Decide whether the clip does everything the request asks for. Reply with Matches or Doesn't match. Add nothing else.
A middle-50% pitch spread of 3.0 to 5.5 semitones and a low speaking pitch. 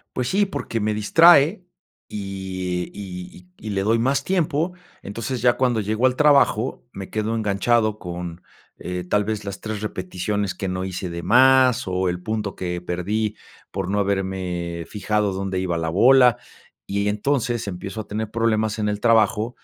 Matches